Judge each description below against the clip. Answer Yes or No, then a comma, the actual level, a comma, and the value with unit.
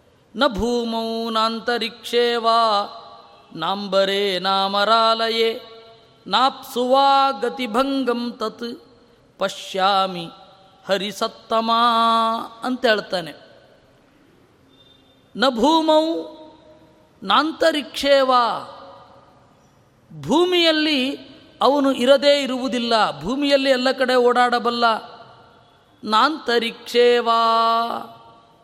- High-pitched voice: Yes, high, 235 Hz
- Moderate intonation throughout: Yes, average, 3.5 semitones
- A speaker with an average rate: No, slow, 50 wpm